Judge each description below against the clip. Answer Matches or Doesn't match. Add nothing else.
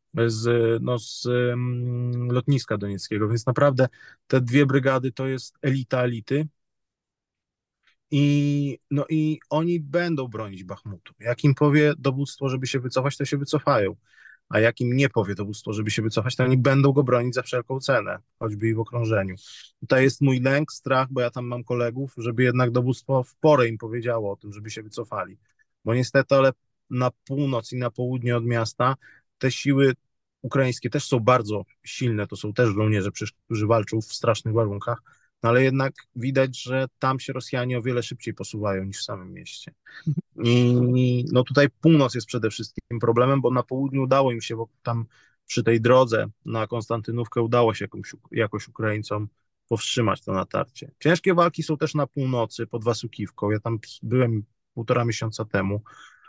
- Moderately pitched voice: Doesn't match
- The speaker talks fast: Matches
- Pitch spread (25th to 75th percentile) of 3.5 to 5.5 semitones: Doesn't match